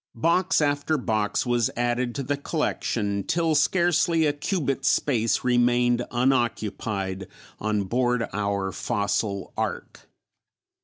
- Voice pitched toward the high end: No, low, 120 Hz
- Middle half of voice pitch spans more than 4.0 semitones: Yes, wide, 5.4 semitones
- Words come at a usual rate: No, slow, 110 wpm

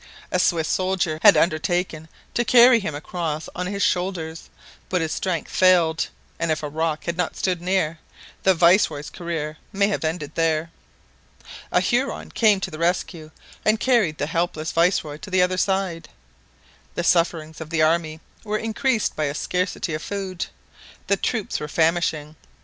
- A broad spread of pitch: No, average, 3.2 semitones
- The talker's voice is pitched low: No, medium, 170 Hz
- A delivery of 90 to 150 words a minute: No, average, 165 wpm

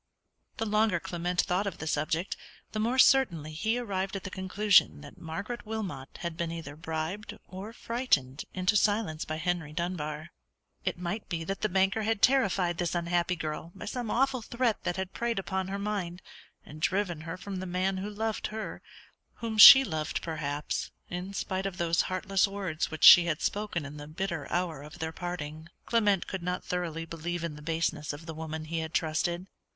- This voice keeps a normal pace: Yes, average, 190 wpm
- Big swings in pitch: No, average, 3.9 semitones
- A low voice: No, medium, 180 Hz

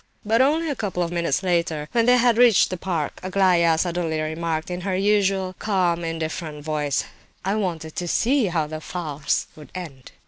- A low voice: No, medium, 175 Hz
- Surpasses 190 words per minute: No, average, 180 wpm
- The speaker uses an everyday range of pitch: Yes, average, 3.7 semitones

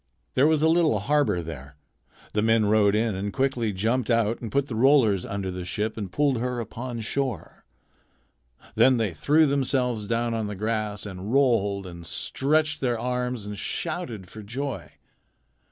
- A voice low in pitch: Yes, low, 115 Hz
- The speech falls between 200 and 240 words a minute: No, average, 170 wpm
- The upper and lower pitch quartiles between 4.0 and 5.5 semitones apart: Yes, average, 4.5 semitones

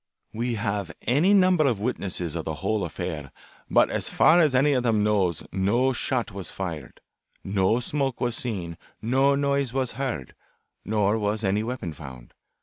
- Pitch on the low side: Yes, low, 110 Hz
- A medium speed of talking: Yes, average, 165 wpm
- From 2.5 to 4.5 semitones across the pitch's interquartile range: No, wide, 5.5 semitones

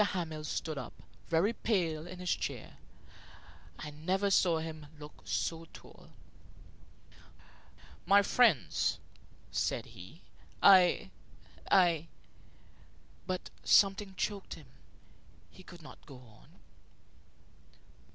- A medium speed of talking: No, slow, 105 wpm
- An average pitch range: Yes, average, 3.8 semitones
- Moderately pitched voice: Yes, medium, 170 Hz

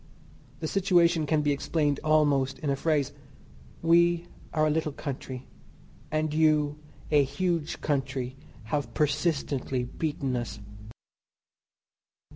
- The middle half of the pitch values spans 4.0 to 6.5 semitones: No, narrow, 2.5 semitones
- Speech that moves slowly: Yes, slow, 110 wpm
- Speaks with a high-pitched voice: No, medium, 150 Hz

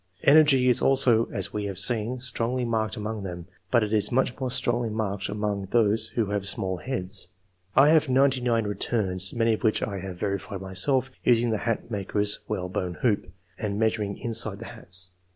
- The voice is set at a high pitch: No, low, 110 Hz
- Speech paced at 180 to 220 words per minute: Yes, average, 195 wpm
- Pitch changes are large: No, average, 3.4 semitones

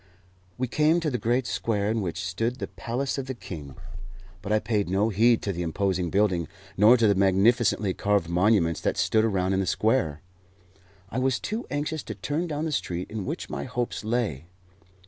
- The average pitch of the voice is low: Yes, low, 105 Hz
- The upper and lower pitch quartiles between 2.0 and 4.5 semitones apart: No, average, 4.9 semitones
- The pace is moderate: Yes, average, 195 wpm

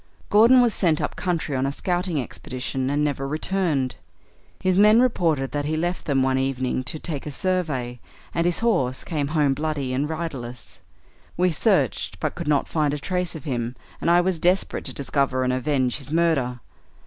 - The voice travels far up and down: No, average, 4.7 semitones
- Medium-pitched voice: Yes, medium, 150 Hz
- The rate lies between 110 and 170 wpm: No, average, 190 wpm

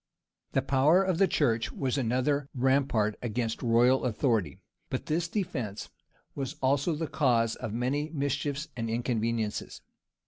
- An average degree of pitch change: Yes, average, 4.0 semitones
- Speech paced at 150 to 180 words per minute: No, average, 140 wpm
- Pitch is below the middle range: Yes, low, 130 Hz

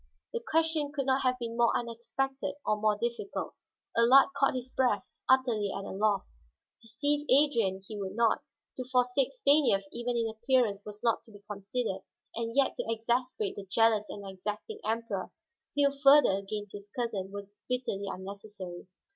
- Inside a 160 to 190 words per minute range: Yes, average, 165 wpm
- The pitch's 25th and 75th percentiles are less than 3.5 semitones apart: No, average, 4.2 semitones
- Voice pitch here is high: Yes, high, 230 Hz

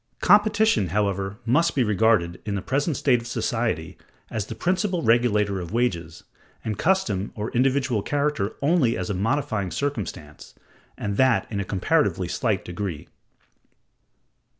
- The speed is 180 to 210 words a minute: No, average, 140 wpm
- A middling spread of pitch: No, wide, 5.9 semitones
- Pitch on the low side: Yes, low, 110 Hz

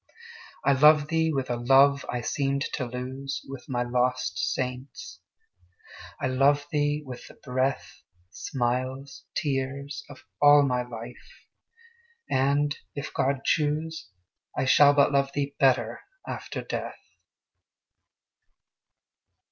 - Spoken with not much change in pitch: Yes, narrow, 2.1 semitones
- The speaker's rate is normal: No, slow, 115 wpm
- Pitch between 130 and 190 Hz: Yes, low, 135 Hz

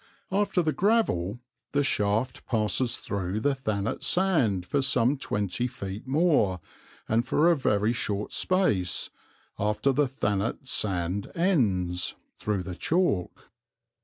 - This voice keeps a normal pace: No, slow, 125 wpm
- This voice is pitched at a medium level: No, low, 115 Hz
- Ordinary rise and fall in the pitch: No, wide, 6.4 semitones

